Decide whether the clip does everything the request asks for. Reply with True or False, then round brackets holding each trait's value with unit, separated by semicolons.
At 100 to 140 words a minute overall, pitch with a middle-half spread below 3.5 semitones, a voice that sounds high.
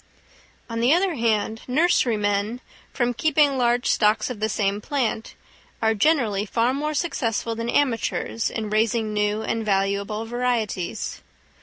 True (135 wpm; 2.9 semitones; 225 Hz)